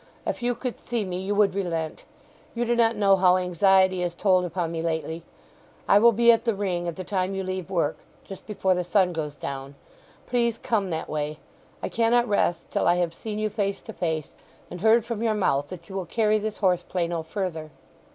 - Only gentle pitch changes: No, average, 3.9 semitones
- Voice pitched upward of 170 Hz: Yes, high, 190 Hz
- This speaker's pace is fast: Yes, fast, 215 wpm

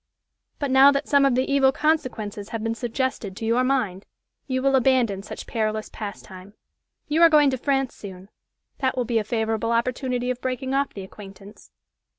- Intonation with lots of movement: No, average, 3.8 semitones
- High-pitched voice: Yes, high, 245 Hz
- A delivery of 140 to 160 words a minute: No, average, 180 wpm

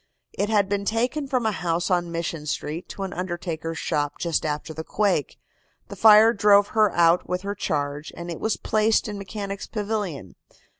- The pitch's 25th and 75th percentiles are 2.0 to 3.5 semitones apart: No, average, 4.2 semitones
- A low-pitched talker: No, high, 190 Hz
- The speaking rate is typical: Yes, average, 185 wpm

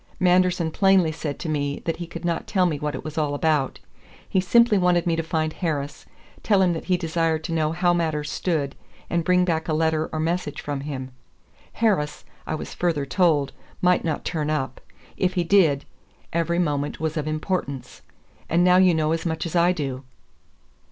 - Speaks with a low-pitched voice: No, medium, 160 Hz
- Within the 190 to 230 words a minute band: Yes, average, 195 wpm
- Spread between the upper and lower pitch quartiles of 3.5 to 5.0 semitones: No, average, 2.8 semitones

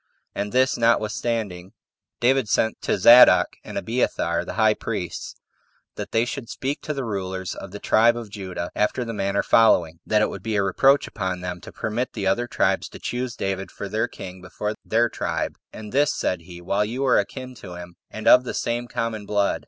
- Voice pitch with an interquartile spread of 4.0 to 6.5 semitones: No, average, 3.6 semitones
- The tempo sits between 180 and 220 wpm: Yes, average, 200 wpm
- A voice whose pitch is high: No, low, 110 Hz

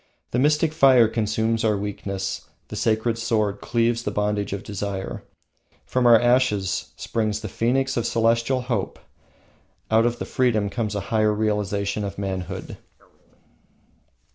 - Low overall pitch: Yes, low, 110 Hz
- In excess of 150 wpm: No, average, 140 wpm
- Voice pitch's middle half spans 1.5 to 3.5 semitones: Yes, average, 2.8 semitones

